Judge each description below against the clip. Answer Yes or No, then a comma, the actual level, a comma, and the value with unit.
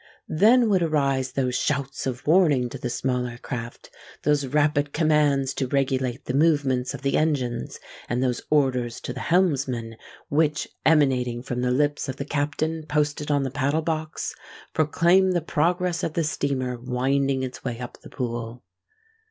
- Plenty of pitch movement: No, average, 3.3 semitones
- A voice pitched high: No, medium, 140 Hz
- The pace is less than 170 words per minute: Yes, average, 155 wpm